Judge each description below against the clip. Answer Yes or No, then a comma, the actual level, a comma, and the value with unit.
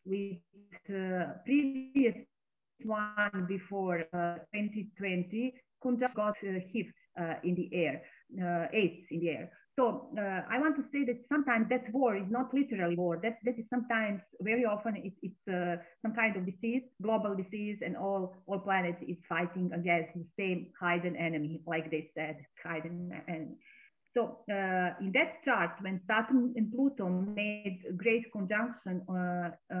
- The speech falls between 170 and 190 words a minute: No, average, 160 wpm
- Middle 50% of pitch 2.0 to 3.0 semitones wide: No, average, 4.6 semitones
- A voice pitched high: Yes, high, 195 Hz